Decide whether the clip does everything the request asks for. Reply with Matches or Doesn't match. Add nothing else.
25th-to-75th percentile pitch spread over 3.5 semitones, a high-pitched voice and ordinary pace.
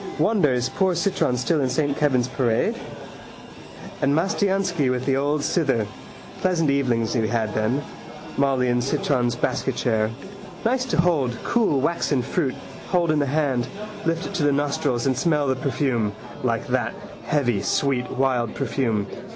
Doesn't match